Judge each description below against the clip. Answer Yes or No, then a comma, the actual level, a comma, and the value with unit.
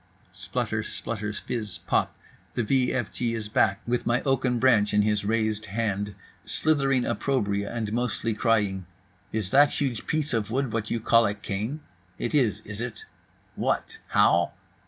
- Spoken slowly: No, average, 155 wpm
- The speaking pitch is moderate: No, low, 115 Hz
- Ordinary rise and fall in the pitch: Yes, average, 3.1 semitones